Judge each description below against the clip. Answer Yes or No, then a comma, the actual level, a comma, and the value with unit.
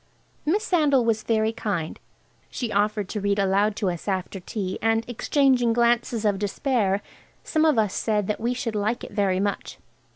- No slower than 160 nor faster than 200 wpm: Yes, average, 170 wpm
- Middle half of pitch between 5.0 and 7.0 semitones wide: No, average, 3.0 semitones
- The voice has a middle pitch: No, high, 215 Hz